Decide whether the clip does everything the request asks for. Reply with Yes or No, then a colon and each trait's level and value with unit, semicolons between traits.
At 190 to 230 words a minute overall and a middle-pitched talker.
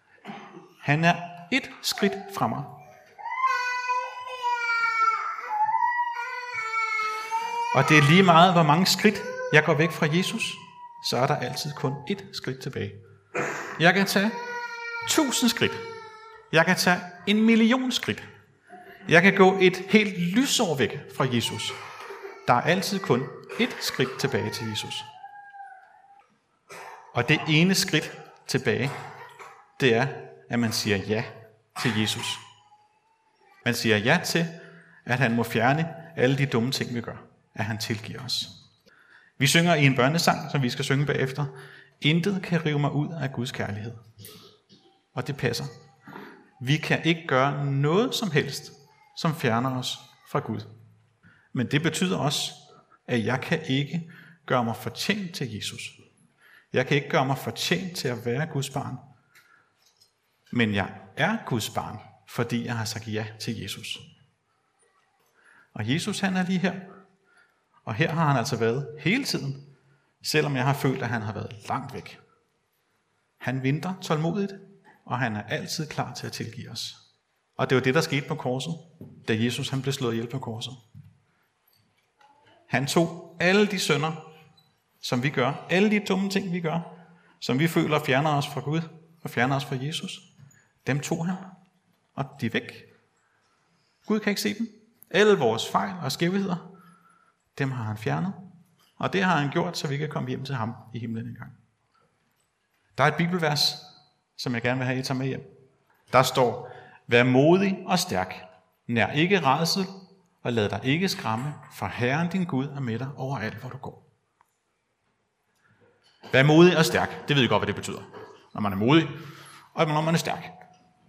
No: average, 165 wpm; medium, 155 Hz